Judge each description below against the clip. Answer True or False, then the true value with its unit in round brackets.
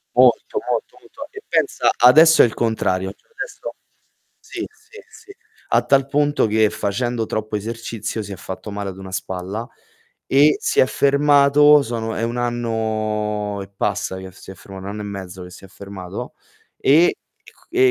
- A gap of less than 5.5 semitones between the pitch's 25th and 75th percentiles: False (5.8 semitones)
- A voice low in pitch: True (110 Hz)